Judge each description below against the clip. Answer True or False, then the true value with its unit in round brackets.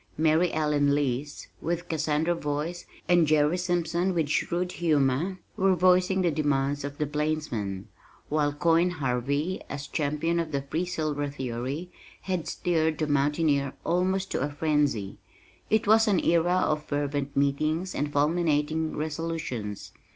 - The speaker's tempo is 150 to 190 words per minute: False (140 wpm)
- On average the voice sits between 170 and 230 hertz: False (155 Hz)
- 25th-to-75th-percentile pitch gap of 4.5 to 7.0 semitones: False (3.1 semitones)